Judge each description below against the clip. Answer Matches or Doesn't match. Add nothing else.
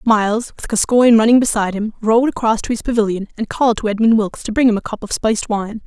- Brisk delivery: Matches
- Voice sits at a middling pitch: Doesn't match